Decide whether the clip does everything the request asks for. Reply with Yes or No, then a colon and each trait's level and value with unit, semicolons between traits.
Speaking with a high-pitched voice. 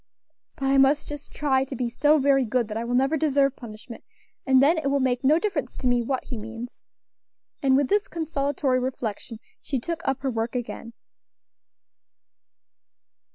Yes: very high, 265 Hz